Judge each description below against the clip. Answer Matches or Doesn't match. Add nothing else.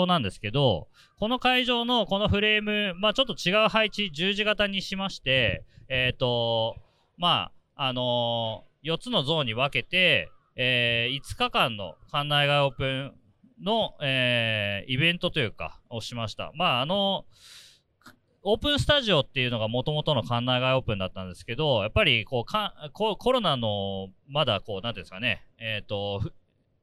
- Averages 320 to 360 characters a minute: Matches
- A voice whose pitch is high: Doesn't match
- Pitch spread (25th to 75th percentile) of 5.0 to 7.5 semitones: Doesn't match